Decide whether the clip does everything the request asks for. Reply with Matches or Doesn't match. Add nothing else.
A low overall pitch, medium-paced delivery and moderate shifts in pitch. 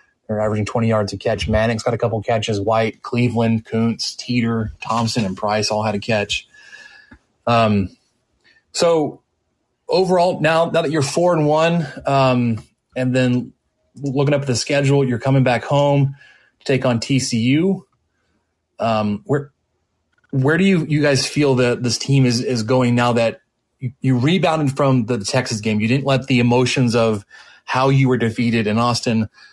Matches